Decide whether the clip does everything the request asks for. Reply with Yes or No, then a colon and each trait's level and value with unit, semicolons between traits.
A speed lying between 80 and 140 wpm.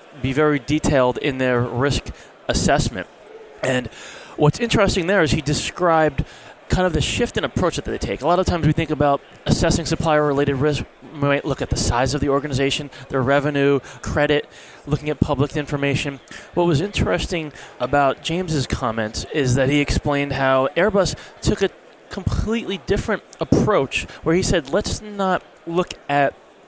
No: average, 165 wpm